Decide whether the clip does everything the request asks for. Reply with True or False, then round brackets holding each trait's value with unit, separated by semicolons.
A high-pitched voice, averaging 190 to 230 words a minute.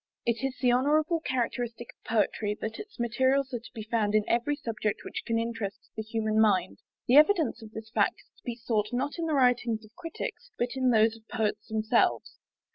True (235 Hz; 205 wpm)